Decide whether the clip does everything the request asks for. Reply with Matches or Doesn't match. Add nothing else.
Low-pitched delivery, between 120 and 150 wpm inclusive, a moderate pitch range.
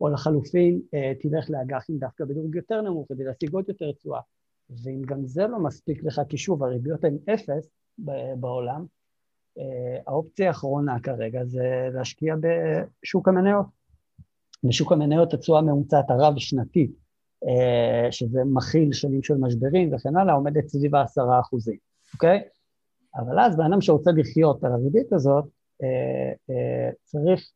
Doesn't match